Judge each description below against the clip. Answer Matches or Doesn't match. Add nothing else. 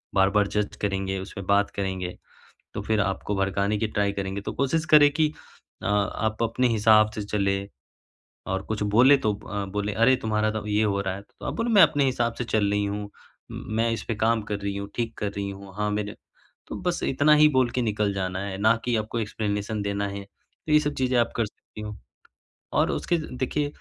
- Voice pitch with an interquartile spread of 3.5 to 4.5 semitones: Doesn't match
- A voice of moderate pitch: Doesn't match